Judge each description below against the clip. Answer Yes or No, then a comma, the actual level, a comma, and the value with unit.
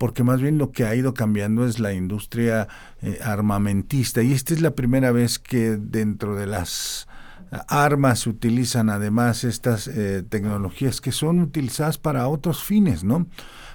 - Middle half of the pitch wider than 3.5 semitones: Yes, average, 4.2 semitones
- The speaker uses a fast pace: No, average, 160 wpm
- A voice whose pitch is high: No, low, 120 Hz